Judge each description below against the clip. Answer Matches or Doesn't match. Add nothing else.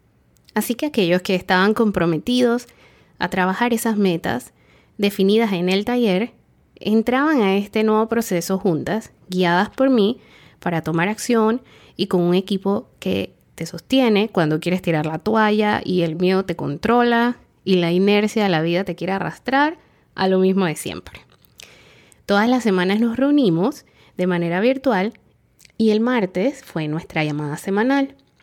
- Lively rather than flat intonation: Doesn't match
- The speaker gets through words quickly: Doesn't match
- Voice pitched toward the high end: Matches